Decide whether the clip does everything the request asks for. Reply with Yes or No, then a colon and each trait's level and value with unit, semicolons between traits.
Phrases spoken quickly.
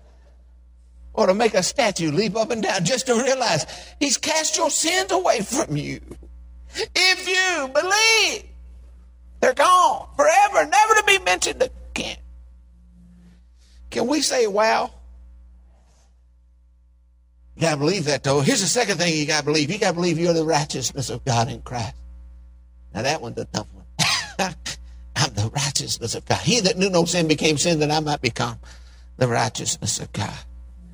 No: average, 165 wpm